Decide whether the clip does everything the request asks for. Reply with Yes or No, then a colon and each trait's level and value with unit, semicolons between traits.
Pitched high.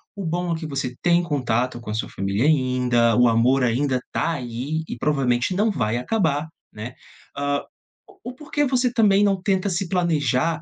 No: medium, 145 Hz